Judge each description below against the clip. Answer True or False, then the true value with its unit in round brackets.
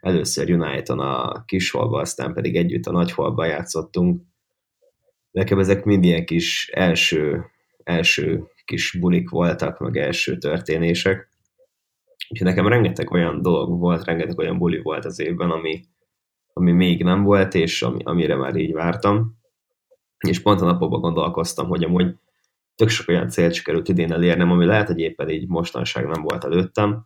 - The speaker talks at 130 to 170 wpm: True (155 wpm)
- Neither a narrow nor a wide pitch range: True (3.3 semitones)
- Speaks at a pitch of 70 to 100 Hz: True (90 Hz)